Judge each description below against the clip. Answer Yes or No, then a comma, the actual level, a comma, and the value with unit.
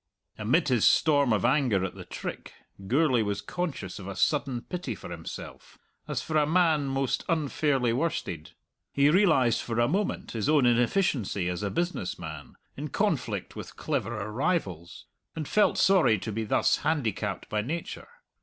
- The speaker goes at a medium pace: Yes, average, 165 wpm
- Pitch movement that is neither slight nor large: No, wide, 6.9 semitones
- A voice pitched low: Yes, low, 130 Hz